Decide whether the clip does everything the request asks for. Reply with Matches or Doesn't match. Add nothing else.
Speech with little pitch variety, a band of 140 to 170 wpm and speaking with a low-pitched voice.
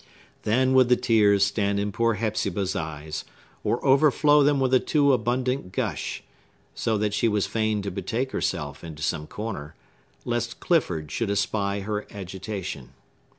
Doesn't match